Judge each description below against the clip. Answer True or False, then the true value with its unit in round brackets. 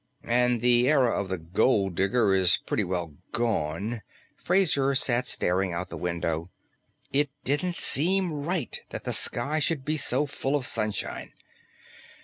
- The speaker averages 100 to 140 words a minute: False (150 wpm)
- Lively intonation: True (7.4 semitones)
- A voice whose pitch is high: False (120 Hz)